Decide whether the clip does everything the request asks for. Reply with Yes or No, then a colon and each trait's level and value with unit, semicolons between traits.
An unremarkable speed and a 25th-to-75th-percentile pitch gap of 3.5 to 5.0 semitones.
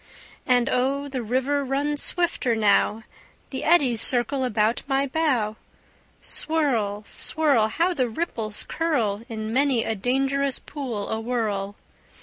No: slow, 125 wpm; average, 4.3 semitones